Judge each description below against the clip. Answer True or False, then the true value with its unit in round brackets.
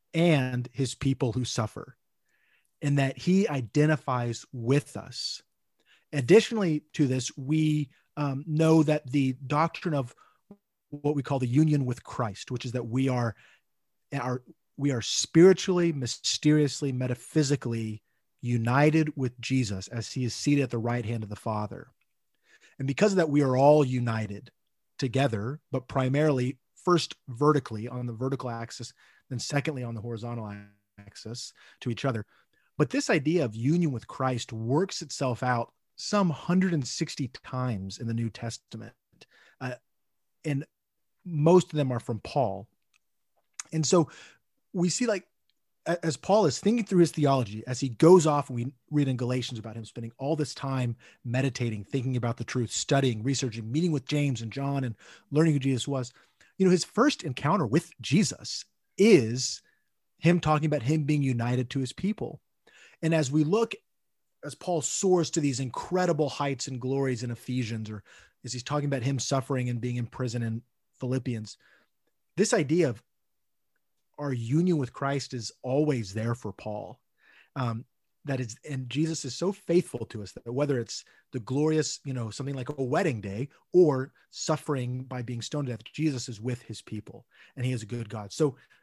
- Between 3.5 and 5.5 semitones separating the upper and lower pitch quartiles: True (4.2 semitones)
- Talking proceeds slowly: False (165 wpm)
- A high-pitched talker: False (135 Hz)